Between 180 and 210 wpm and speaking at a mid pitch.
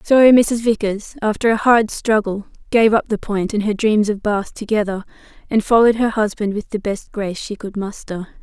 No: average, 200 wpm; high, 215 Hz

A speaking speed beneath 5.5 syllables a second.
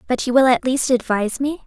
No: 6.0 syllables/s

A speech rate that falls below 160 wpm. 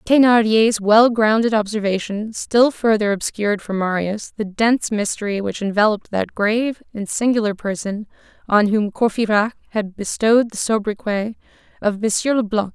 Yes: slow, 135 wpm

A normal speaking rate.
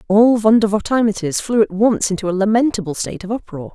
Yes: average, 175 wpm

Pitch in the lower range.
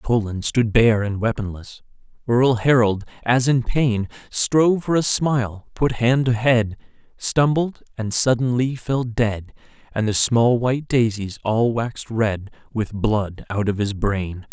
Yes: low, 115 Hz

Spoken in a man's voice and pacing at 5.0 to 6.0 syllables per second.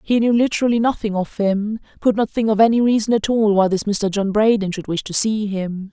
No: female; 5.5 syllables/s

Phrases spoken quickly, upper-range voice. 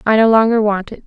Yes: fast, 280 wpm; high, 215 Hz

